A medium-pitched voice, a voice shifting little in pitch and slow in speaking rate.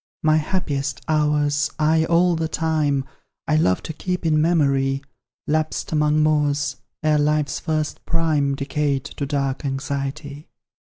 Yes: medium, 150 Hz; narrow, 1.9 semitones; slow, 130 wpm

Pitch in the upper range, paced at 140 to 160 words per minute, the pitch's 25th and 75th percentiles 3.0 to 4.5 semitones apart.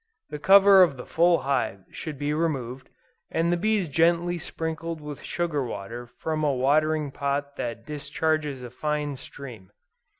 No: medium, 150 Hz; average, 155 wpm; average, 3.5 semitones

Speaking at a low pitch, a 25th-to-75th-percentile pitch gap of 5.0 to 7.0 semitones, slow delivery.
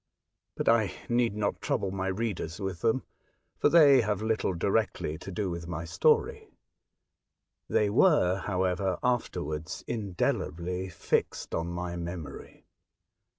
No: very low, 95 Hz; average, 3.9 semitones; slow, 125 wpm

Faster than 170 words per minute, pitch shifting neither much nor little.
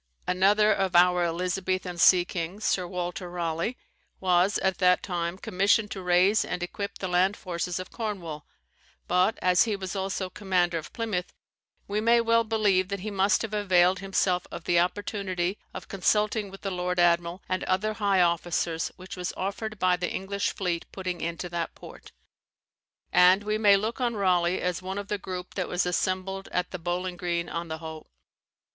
No: average, 180 wpm; narrow, 2.1 semitones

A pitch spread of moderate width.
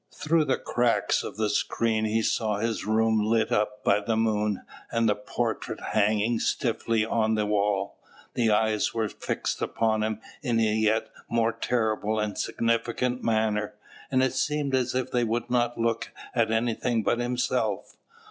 No: narrow, 1.7 semitones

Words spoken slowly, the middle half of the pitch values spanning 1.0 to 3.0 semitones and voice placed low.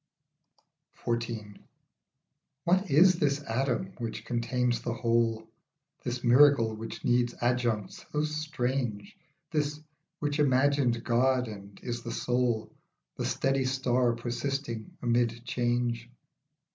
Yes: slow, 105 wpm; average, 2.7 semitones; low, 120 Hz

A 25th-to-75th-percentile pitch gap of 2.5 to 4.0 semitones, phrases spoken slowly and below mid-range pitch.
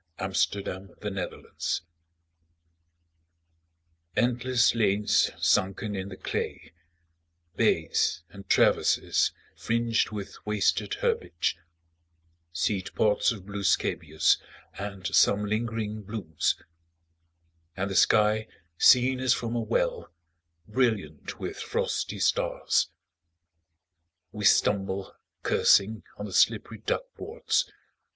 Yes: average, 2.8 semitones; slow, 100 wpm; low, 105 Hz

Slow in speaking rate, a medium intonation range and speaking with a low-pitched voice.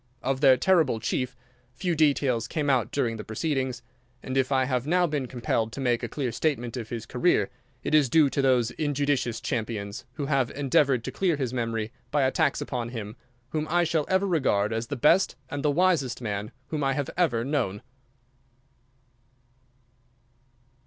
No: average, 175 wpm; average, 4.1 semitones; low, 130 Hz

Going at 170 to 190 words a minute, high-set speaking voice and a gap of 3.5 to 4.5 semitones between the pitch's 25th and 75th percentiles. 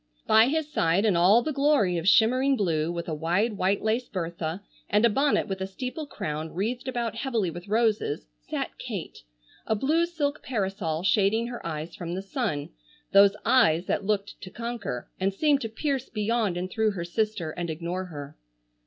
No: average, 185 wpm; high, 205 Hz; wide, 5.4 semitones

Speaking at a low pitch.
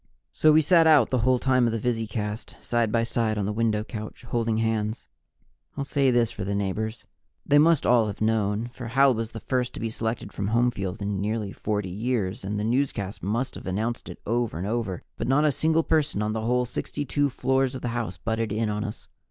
Yes: low, 115 Hz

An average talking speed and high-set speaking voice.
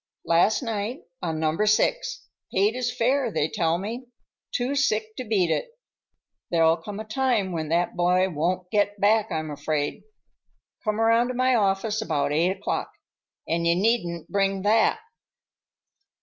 Yes: average, 150 wpm; high, 205 Hz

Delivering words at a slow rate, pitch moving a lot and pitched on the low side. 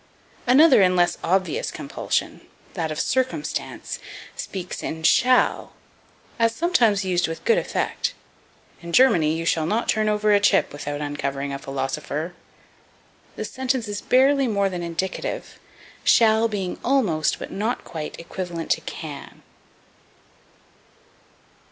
No: slow, 125 wpm; wide, 6.1 semitones; high, 190 Hz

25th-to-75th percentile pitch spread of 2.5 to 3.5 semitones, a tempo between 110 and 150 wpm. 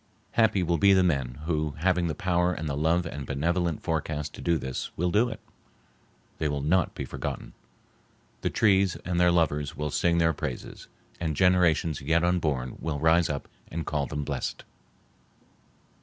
No: average, 3.0 semitones; average, 170 wpm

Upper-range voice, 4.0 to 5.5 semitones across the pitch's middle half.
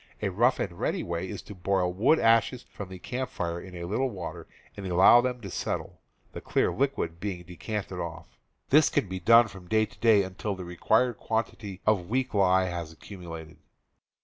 No: very low, 95 Hz; average, 4.3 semitones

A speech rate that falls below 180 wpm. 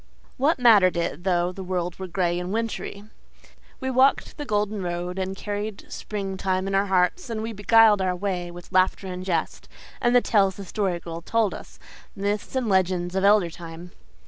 No: average, 190 wpm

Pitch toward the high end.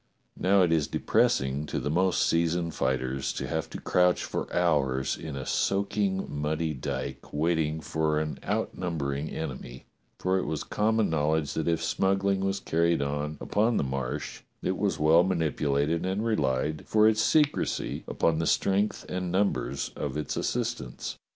No: very low, 80 Hz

